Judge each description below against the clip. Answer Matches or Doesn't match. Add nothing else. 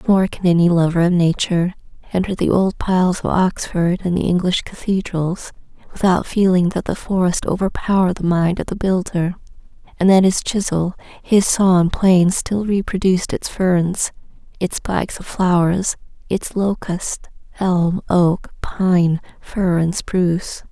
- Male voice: Doesn't match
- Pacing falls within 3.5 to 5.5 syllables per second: Matches